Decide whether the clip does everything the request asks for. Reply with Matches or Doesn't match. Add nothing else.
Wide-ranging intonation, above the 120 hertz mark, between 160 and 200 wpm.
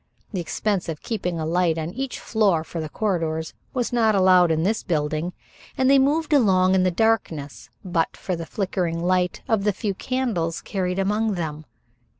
Doesn't match